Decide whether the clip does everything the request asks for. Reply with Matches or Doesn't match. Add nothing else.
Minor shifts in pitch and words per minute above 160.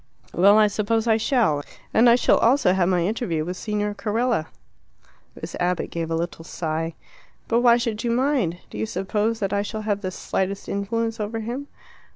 Doesn't match